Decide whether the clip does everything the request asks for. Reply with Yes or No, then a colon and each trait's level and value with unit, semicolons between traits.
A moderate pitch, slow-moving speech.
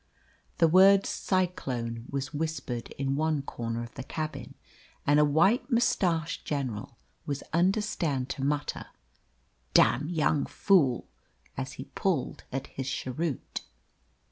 Yes: medium, 145 Hz; slow, 120 wpm